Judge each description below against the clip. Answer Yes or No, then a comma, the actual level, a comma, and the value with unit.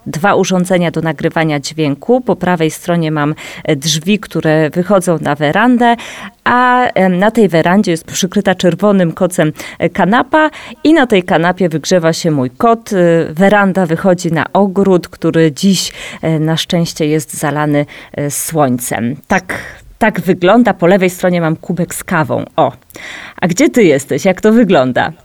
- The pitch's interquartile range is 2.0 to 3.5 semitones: No, average, 3.9 semitones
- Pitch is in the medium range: Yes, medium, 180 Hz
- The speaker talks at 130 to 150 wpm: Yes, average, 145 wpm